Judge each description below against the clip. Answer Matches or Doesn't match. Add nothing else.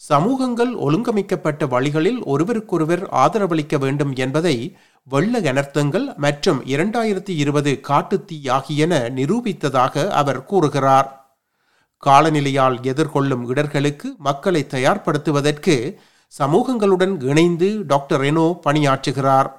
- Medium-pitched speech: Matches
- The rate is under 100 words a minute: Matches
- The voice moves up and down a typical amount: Matches